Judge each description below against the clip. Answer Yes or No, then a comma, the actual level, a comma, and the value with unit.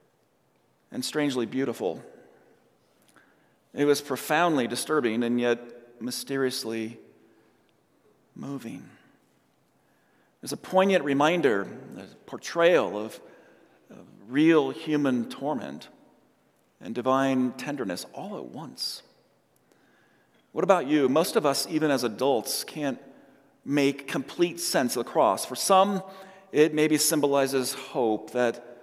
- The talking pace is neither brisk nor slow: No, slow, 105 wpm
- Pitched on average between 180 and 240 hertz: No, medium, 140 Hz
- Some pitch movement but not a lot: Yes, average, 4.0 semitones